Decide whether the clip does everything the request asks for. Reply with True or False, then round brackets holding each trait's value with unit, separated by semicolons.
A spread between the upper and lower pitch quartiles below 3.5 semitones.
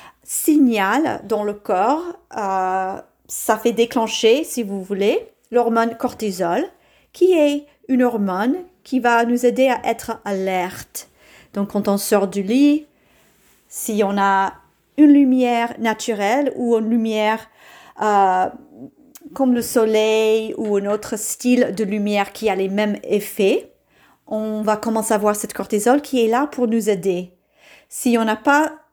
False (4.2 semitones)